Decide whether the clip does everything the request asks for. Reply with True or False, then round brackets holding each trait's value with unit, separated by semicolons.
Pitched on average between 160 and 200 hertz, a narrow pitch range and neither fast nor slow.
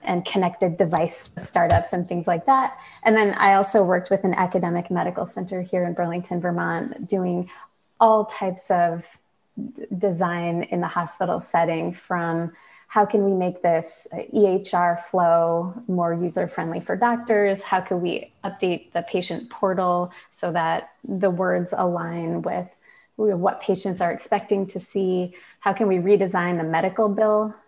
True (185 Hz; 2.3 semitones; 150 wpm)